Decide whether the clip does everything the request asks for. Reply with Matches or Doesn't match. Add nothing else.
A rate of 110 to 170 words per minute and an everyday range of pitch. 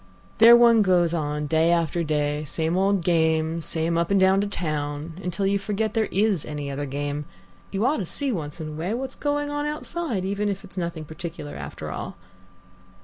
Doesn't match